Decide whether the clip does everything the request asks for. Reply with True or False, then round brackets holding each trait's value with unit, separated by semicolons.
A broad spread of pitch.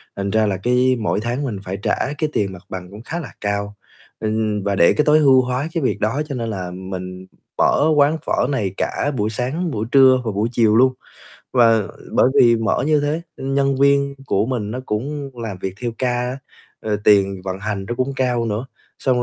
False (4.6 semitones)